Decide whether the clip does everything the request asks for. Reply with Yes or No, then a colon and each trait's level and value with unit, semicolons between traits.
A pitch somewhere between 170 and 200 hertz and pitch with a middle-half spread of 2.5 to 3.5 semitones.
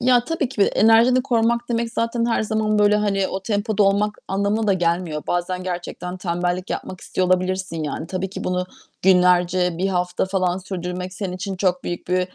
Yes: high, 190 Hz; average, 2.9 semitones